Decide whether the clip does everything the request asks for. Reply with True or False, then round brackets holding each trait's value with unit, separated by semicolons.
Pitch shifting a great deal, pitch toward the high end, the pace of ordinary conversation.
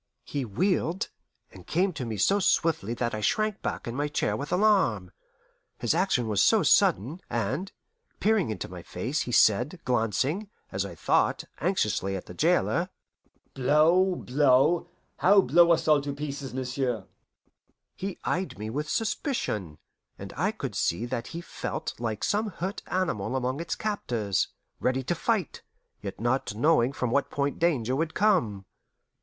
False (7.6 semitones; 140 Hz; 160 wpm)